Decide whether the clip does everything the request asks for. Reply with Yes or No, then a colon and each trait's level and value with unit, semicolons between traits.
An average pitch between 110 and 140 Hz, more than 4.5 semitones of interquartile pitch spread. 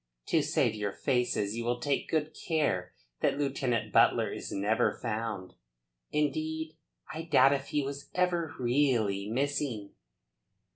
Yes: low, 135 Hz; average, 5.2 semitones